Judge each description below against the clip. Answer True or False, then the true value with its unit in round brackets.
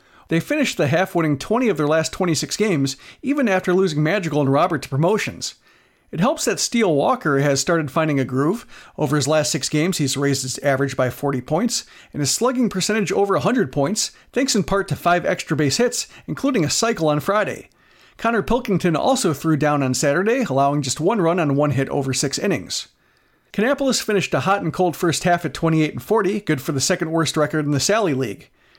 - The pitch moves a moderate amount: False (5.7 semitones)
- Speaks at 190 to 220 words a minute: True (200 wpm)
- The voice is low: False (165 Hz)